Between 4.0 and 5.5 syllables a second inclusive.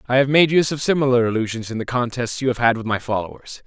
No: 6.9 syllables/s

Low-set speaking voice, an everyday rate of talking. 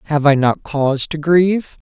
No: medium, 155 Hz; average, 185 wpm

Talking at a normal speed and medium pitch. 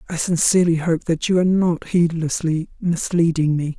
Yes: average, 160 wpm; medium, 170 Hz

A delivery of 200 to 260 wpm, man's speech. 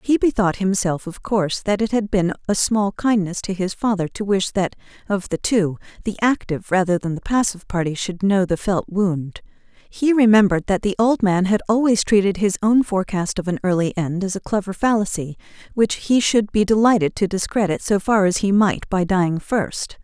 No: fast, 205 wpm; female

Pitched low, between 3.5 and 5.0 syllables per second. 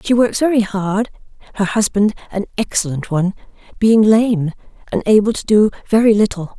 No: high, 210 Hz; 4.6 syllables/s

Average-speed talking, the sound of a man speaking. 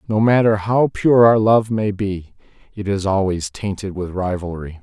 Yes: average, 175 wpm; male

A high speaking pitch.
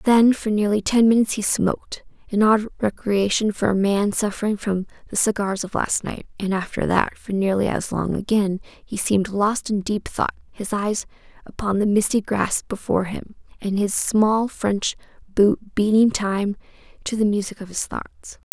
Yes: high, 205 Hz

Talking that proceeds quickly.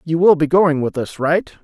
Yes: fast, 255 wpm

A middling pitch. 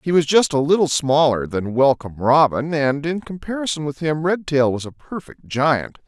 Yes: medium, 145 Hz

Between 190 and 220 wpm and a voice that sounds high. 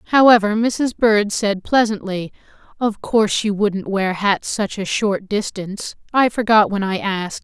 No: average, 155 wpm; high, 205 Hz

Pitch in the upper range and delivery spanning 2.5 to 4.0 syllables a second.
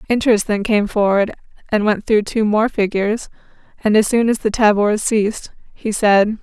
No: high, 215 Hz; 5.0 syllables/s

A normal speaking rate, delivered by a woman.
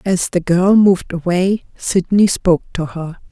Yes: average, 165 wpm; female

